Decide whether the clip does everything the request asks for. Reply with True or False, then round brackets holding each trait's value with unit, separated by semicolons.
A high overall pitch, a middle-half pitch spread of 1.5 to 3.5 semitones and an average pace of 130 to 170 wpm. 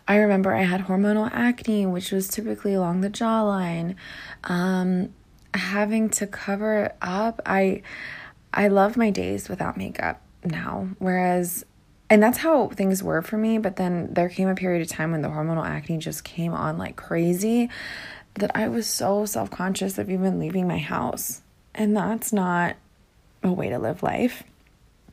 True (195 Hz; 3.1 semitones; 165 wpm)